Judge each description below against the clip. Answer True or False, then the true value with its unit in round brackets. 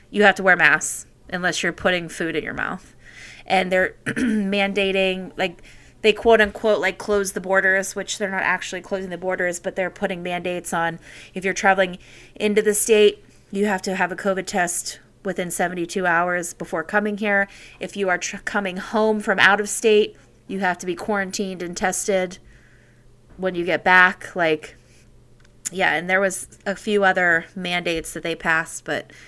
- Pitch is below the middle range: False (185 Hz)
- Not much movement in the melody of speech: True (2.3 semitones)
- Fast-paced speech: False (180 wpm)